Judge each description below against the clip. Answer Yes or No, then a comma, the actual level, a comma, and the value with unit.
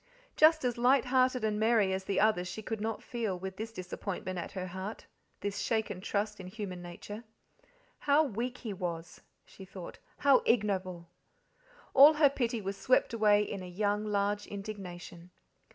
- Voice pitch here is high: Yes, high, 205 Hz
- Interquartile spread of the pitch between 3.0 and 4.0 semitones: Yes, average, 3.7 semitones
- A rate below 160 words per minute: No, average, 170 wpm